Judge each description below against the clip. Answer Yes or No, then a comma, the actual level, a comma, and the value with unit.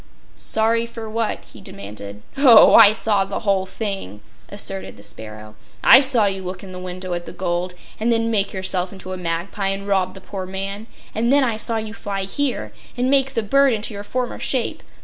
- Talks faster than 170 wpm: Yes, fast, 205 wpm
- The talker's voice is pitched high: Yes, high, 200 Hz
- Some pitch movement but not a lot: Yes, average, 3.8 semitones